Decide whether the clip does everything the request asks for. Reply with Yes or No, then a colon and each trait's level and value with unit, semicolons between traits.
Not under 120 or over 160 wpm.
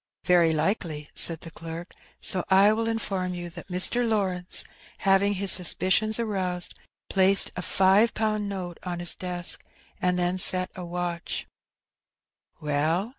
Yes: average, 145 wpm